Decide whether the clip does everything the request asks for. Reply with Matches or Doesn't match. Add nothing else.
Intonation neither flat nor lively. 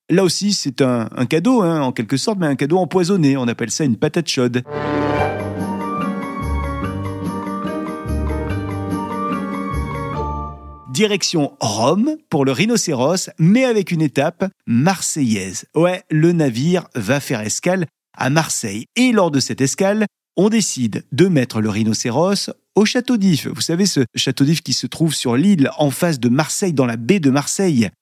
Doesn't match